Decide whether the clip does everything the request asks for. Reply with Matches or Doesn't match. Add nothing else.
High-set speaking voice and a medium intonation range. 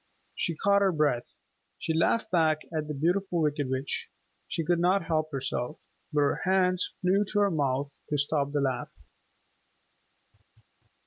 Doesn't match